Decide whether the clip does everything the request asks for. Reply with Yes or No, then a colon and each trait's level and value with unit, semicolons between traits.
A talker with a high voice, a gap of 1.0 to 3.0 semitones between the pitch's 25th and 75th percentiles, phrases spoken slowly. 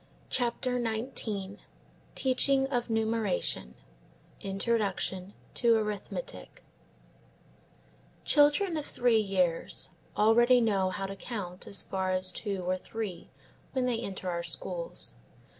No: high, 215 Hz; average, 4.3 semitones; slow, 110 wpm